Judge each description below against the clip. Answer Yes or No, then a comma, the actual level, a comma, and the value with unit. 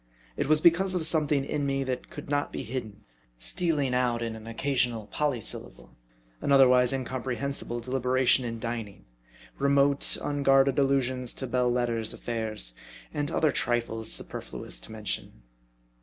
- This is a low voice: Yes, low, 130 Hz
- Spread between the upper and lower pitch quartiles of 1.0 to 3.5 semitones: Yes, average, 3.0 semitones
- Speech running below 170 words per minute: Yes, average, 140 wpm